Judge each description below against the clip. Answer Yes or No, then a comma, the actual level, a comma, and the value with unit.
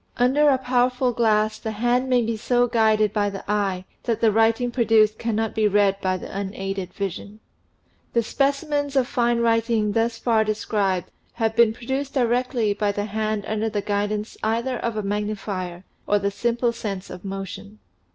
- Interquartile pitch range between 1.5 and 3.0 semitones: Yes, narrow, 2.6 semitones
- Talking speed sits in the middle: Yes, average, 170 wpm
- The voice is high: Yes, high, 220 Hz